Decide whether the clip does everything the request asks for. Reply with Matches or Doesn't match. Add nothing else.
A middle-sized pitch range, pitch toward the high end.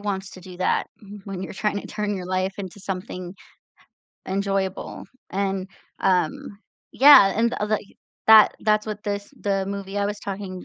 Doesn't match